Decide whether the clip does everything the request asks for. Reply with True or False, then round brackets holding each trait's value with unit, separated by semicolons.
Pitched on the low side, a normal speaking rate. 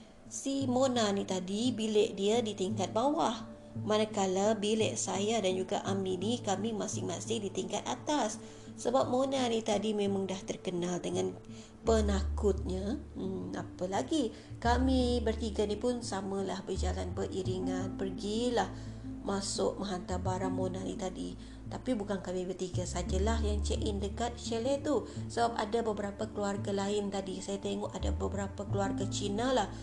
False (195 Hz; 145 wpm)